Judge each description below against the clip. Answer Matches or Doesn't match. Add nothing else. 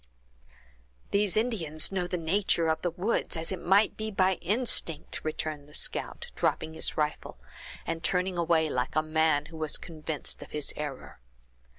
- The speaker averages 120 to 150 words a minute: Doesn't match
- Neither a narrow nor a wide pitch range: Matches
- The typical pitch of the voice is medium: Matches